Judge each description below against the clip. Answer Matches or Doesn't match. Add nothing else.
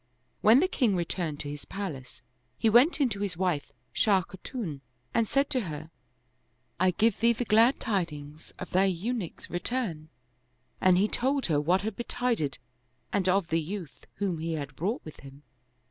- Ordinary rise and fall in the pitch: Doesn't match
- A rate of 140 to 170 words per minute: Doesn't match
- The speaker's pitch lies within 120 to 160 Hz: Doesn't match